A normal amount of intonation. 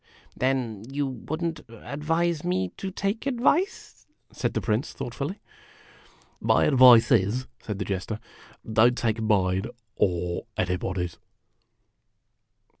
No: wide, 7.0 semitones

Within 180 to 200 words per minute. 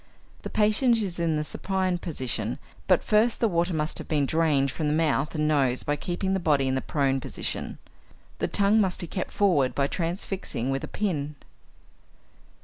Yes: average, 185 wpm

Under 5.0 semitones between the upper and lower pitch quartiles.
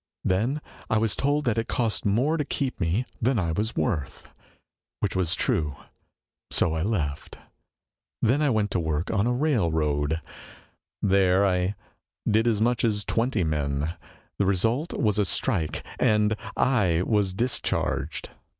No: wide, 5.6 semitones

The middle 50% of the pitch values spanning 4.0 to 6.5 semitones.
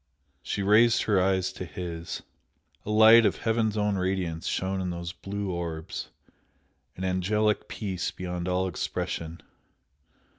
No: average, 2.8 semitones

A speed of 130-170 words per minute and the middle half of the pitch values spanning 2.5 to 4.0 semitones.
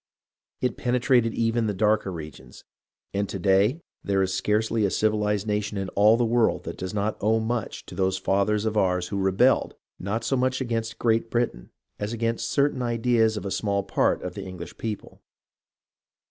No: average, 180 wpm; average, 2.9 semitones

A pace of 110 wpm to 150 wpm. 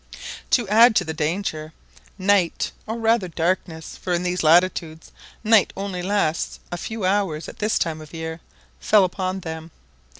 No: average, 160 wpm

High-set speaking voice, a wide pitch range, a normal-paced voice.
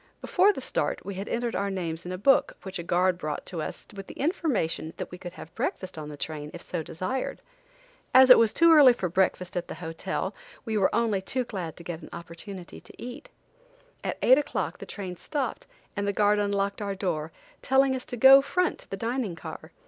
No: high, 195 Hz; wide, 6.0 semitones; fast, 220 wpm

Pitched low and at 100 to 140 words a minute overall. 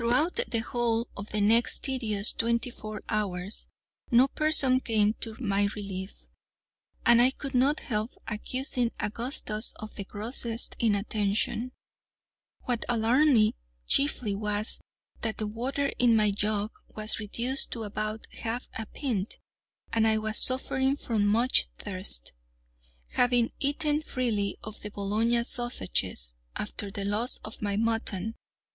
No: high, 225 Hz; slow, 135 wpm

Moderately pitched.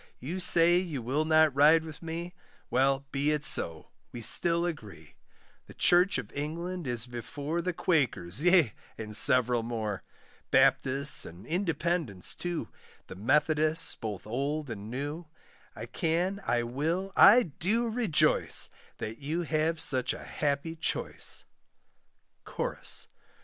Yes: medium, 150 Hz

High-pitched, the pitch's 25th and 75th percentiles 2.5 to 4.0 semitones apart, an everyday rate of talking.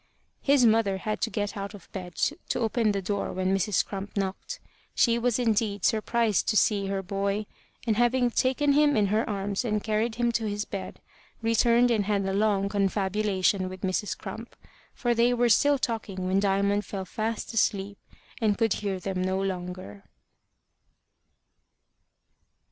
Yes: high, 205 Hz; average, 2.9 semitones; average, 165 wpm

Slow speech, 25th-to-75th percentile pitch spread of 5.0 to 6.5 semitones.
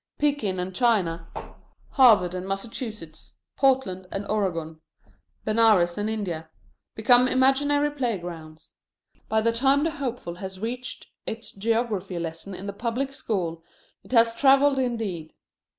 Yes: slow, 125 wpm; wide, 5.6 semitones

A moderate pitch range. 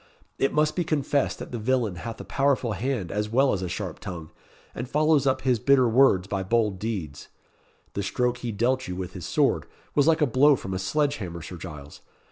No: wide, 6.4 semitones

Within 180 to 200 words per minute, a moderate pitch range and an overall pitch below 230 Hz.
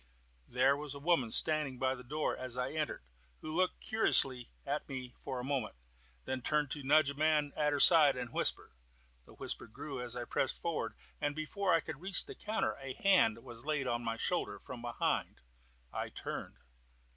Yes: average, 190 wpm; average, 3.6 semitones; medium, 140 Hz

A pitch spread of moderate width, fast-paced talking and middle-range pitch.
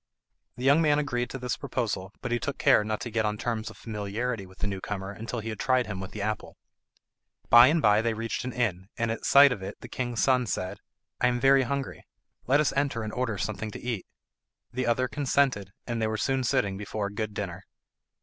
No: average, 3.5 semitones; fast, 230 wpm; low, 115 Hz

